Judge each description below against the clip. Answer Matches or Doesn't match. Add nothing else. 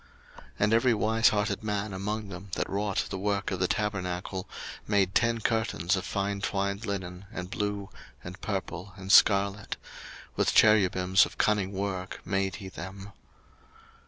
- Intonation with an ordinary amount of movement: Doesn't match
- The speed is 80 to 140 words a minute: Doesn't match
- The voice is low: Matches